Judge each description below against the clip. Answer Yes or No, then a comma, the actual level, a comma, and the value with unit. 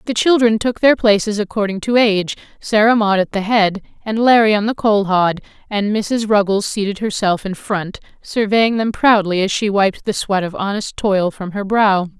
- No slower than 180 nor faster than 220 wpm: Yes, average, 195 wpm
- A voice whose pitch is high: Yes, high, 205 Hz